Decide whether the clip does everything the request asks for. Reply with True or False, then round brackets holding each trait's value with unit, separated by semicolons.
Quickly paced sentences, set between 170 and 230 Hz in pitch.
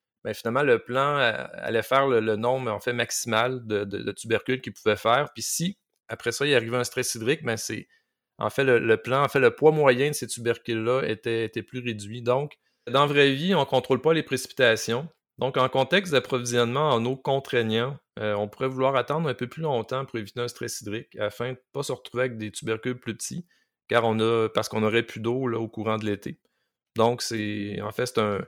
False (230 wpm; 120 Hz)